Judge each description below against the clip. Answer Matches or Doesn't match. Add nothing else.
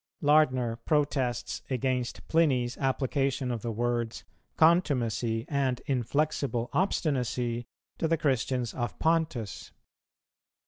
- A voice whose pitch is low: Matches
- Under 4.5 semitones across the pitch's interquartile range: Matches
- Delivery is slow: Matches